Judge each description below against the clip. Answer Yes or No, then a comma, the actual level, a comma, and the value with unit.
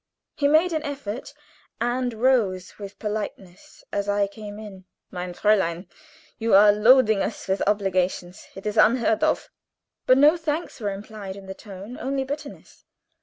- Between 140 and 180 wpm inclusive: Yes, average, 160 wpm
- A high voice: Yes, high, 210 Hz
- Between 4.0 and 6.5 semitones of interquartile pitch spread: Yes, average, 4.6 semitones